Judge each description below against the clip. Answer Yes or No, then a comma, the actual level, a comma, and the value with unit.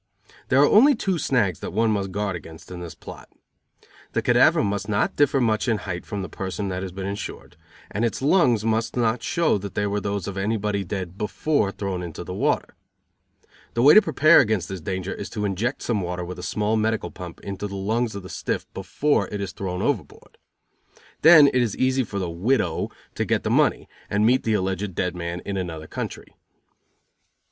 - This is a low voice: Yes, low, 100 Hz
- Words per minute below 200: No, fast, 205 wpm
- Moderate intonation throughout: Yes, average, 3.9 semitones